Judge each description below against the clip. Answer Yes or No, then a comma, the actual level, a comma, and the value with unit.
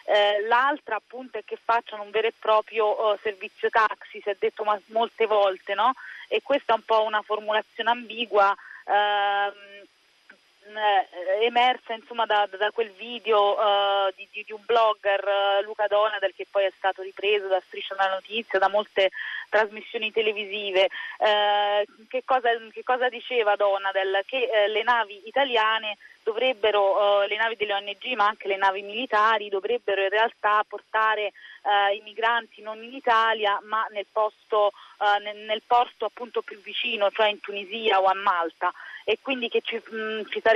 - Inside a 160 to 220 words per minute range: Yes, average, 165 wpm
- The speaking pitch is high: Yes, high, 215 Hz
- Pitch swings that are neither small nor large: No, narrow, 1.9 semitones